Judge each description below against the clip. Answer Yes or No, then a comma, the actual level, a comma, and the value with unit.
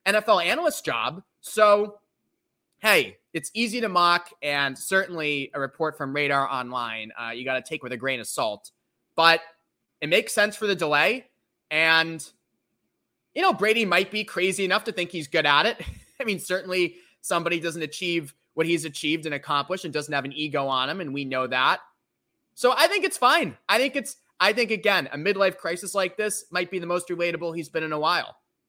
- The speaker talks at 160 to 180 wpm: No, average, 200 wpm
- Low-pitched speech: No, medium, 170 Hz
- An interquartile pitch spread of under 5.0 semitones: No, wide, 5.6 semitones